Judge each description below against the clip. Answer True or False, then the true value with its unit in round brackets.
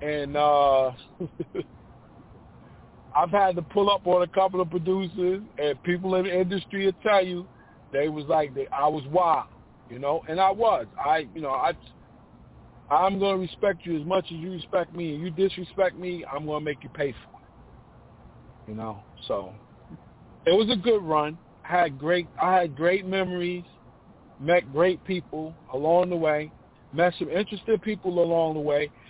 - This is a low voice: False (175 Hz)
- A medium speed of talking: True (175 wpm)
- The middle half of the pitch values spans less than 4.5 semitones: True (3.9 semitones)